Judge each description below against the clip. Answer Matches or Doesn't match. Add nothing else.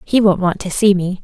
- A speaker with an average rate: Doesn't match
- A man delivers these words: Doesn't match